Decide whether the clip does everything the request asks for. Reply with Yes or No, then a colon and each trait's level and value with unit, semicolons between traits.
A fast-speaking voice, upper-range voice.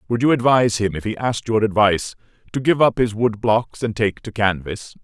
No: fast, 225 wpm; low, 110 Hz